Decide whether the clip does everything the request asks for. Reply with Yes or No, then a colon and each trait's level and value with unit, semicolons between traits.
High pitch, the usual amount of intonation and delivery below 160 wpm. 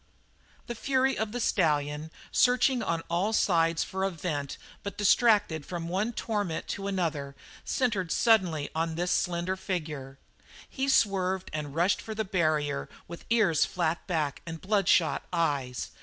No: medium, 175 Hz; average, 4.6 semitones; average, 145 wpm